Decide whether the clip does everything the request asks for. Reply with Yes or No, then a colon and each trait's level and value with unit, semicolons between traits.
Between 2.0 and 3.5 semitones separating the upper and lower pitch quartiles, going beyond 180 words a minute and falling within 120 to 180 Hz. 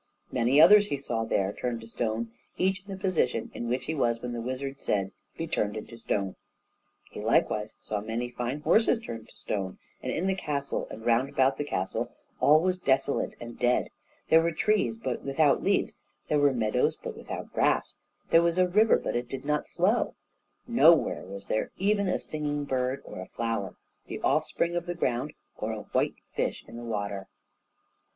No: wide, 6.6 semitones; average, 190 wpm; low, 135 Hz